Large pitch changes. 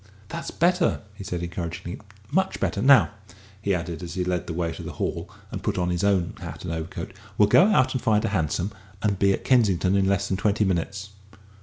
No: average, 3.5 semitones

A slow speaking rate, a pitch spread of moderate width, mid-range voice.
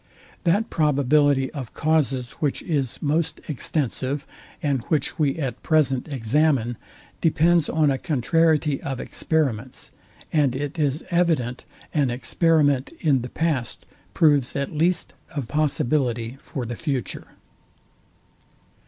Yes: slow, 120 wpm; average, 3.3 semitones; medium, 145 Hz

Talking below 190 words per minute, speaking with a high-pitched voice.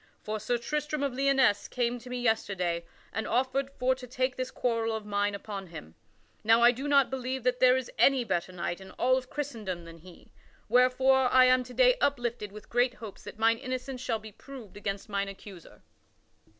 No: average, 200 wpm; high, 245 Hz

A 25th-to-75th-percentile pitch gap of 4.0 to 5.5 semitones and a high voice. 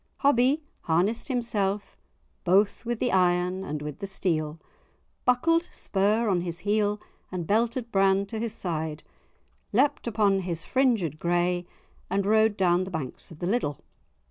Yes: average, 4.5 semitones; high, 195 Hz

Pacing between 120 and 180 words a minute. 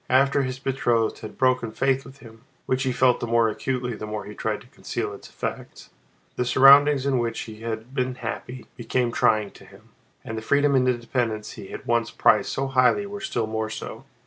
No: average, 200 wpm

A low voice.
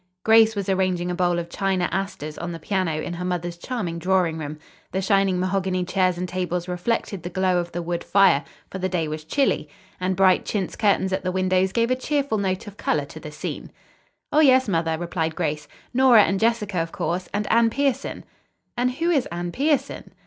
No: medium, 185 Hz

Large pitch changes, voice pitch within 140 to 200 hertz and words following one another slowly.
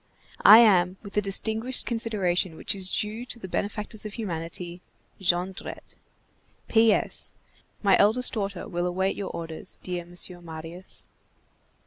No: average, 3.4 semitones; high, 190 Hz; slow, 130 wpm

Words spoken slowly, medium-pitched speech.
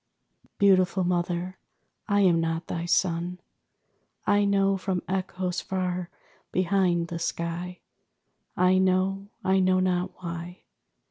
Yes: slow, 115 wpm; medium, 180 Hz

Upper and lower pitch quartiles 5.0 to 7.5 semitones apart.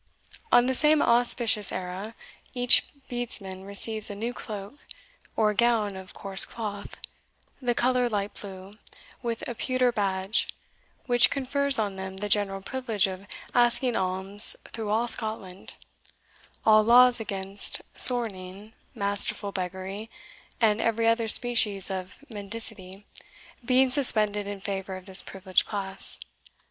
No: average, 3.6 semitones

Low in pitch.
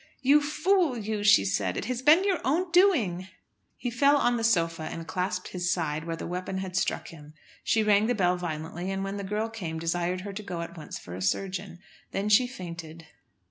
No: high, 190 Hz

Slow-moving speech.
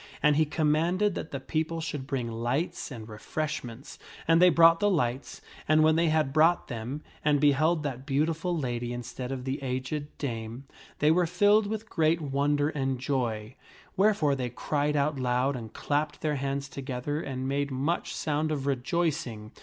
No: average, 170 wpm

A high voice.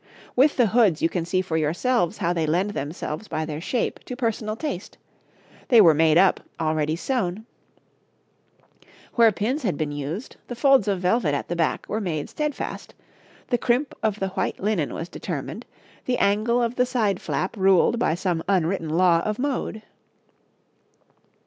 Yes: high, 195 Hz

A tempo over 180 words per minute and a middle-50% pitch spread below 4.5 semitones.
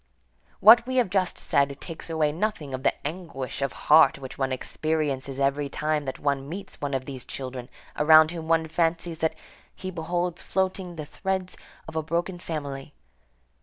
No: average, 170 wpm; average, 3.9 semitones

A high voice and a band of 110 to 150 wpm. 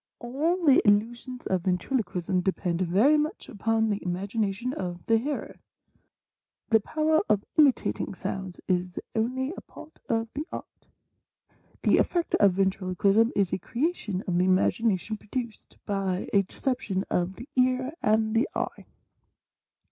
Yes: high, 215 Hz; average, 140 wpm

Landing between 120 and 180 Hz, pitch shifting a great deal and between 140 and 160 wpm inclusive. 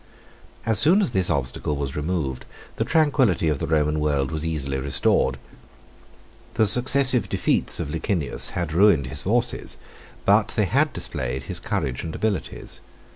No: very low, 80 Hz; wide, 7.2 semitones; average, 150 wpm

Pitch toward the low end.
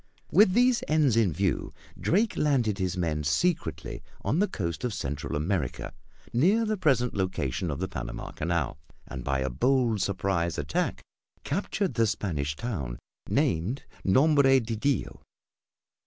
Yes: low, 105 Hz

